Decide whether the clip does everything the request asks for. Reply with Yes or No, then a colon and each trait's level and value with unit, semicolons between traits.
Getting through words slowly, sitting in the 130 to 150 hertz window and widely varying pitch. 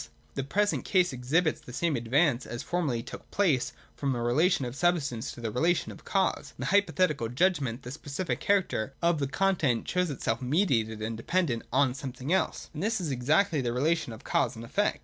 No: average, 195 wpm; medium, 140 Hz; wide, 6.4 semitones